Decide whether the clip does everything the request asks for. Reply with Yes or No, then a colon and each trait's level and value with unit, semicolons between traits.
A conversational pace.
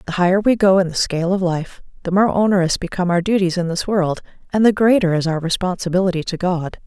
No: fast, 225 wpm